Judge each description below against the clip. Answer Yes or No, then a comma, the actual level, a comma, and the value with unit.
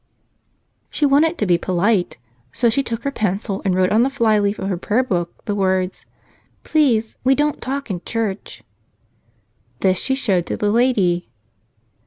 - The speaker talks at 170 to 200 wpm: No, average, 160 wpm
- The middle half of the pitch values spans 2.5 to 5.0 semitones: No, wide, 5.5 semitones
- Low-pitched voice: No, high, 210 Hz